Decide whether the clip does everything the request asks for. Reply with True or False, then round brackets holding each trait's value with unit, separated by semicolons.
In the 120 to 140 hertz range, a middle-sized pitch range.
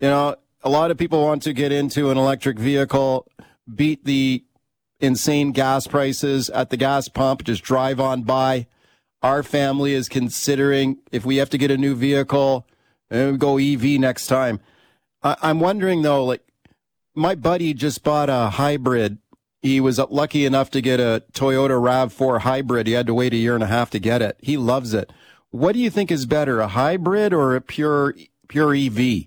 False (135 Hz; 2.0 semitones)